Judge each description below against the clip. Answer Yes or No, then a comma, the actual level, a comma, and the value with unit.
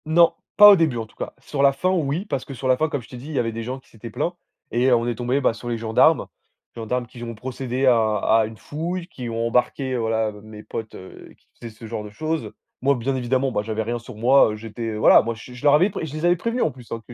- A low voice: Yes, low, 125 Hz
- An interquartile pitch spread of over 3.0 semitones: Yes, average, 3.7 semitones